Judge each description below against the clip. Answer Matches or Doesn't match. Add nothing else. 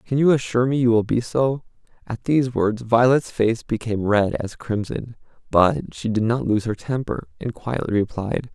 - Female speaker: Doesn't match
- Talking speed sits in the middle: Matches